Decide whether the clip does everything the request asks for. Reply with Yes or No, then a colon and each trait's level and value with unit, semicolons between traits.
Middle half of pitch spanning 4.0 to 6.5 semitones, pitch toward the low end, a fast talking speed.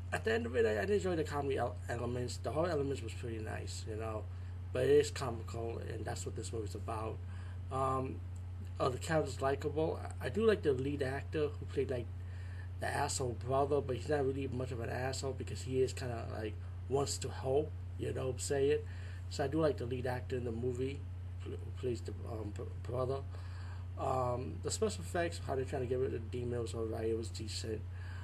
Yes: average, 5.0 semitones; low, 100 Hz; fast, 220 wpm